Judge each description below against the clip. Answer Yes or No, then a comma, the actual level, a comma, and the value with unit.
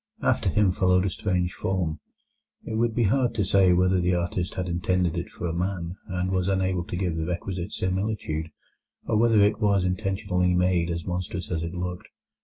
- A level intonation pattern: Yes, narrow, 1.7 semitones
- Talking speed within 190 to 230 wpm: Yes, average, 195 wpm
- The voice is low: Yes, very low, 90 Hz